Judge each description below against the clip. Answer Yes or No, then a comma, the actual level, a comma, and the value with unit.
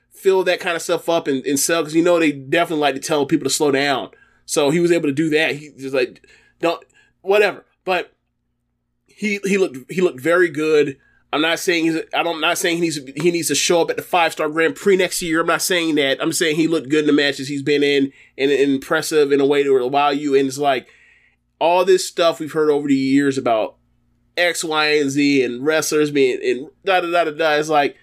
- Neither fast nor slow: No, fast, 250 wpm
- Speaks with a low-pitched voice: No, medium, 155 Hz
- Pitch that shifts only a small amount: No, average, 3.2 semitones